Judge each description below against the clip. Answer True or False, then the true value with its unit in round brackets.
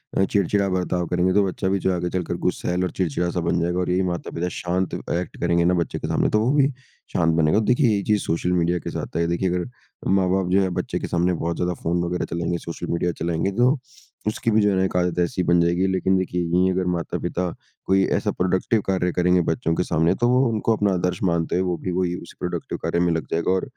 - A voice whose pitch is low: True (90 Hz)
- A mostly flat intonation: True (1.6 semitones)